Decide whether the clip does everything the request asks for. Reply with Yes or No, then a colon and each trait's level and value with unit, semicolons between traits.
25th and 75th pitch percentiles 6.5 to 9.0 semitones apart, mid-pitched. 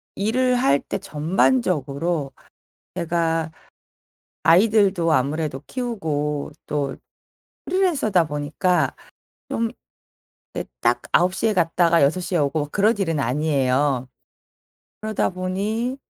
No: wide, 5.6 semitones; medium, 170 Hz